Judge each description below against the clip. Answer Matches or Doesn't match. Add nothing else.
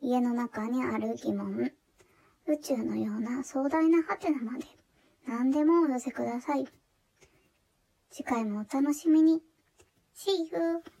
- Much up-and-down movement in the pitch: Doesn't match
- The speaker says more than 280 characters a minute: Doesn't match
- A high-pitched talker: Matches